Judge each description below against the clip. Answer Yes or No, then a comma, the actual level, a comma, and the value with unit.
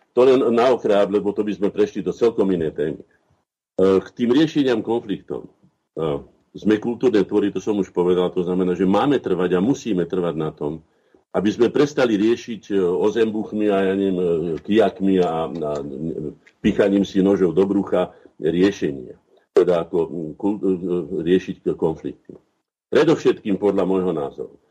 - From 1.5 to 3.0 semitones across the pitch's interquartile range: Yes, narrow, 2.4 semitones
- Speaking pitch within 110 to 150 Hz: No, very low, 95 Hz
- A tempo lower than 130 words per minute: No, average, 140 wpm